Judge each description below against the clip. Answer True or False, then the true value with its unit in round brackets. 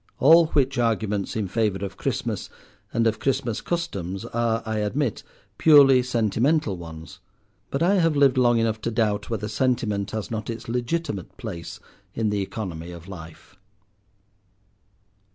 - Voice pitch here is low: True (115 Hz)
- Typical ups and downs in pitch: True (4.3 semitones)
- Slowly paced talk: False (145 wpm)